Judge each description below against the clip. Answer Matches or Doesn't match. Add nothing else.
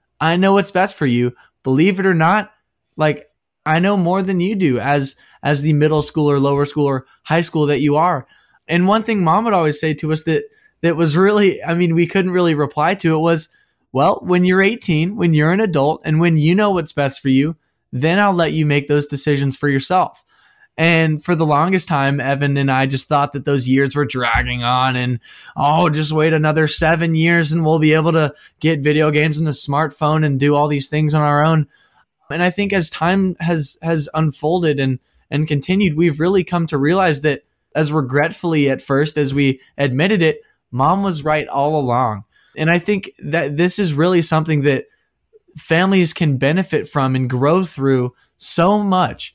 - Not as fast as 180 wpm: Doesn't match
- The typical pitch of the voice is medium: Matches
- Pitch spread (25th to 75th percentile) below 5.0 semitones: Matches